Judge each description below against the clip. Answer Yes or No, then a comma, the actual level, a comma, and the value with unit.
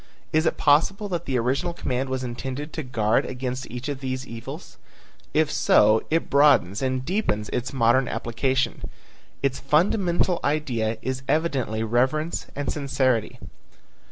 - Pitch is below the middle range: Yes, low, 130 Hz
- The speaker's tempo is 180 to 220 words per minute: No, average, 140 wpm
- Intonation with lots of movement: No, average, 3.7 semitones